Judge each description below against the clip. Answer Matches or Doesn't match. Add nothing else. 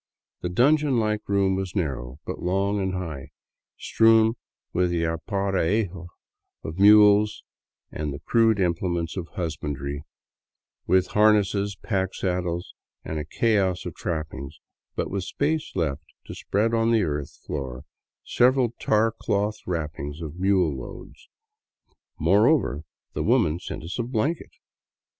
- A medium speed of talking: Doesn't match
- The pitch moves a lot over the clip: Doesn't match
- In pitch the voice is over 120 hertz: Doesn't match